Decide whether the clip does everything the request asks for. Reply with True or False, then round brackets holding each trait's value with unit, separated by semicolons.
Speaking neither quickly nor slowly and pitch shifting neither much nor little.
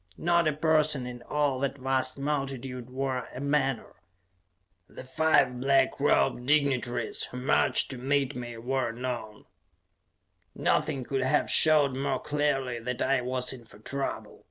False (145 wpm; 2.1 semitones)